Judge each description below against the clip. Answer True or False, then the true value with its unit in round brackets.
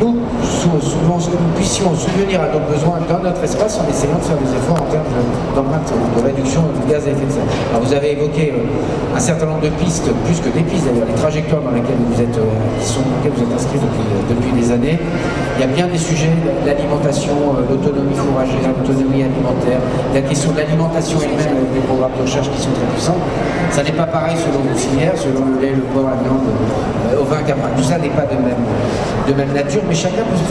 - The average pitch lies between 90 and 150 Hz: True (140 Hz)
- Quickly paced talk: True (225 wpm)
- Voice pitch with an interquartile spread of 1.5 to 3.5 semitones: True (3.0 semitones)